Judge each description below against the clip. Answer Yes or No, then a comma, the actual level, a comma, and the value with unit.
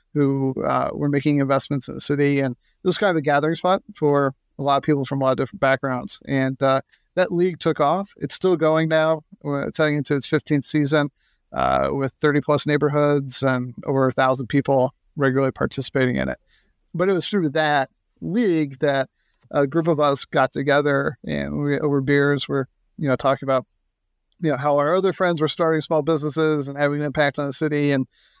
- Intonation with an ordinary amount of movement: No, narrow, 2.3 semitones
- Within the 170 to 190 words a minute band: No, fast, 205 wpm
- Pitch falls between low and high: Yes, medium, 145 Hz